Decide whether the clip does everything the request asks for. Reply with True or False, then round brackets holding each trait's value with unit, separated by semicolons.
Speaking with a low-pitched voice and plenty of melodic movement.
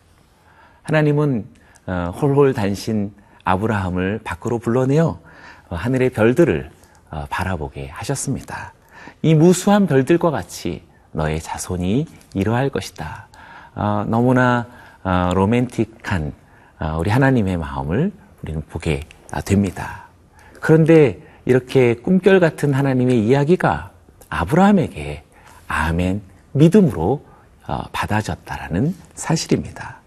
True (110 Hz; 7.4 semitones)